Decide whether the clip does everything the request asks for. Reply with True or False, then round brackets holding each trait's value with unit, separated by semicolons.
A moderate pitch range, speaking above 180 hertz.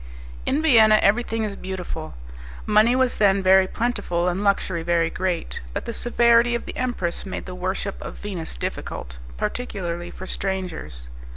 True (4.6 semitones; 190 Hz)